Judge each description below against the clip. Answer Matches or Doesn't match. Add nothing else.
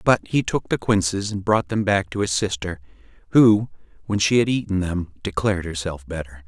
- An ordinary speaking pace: Matches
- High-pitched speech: Doesn't match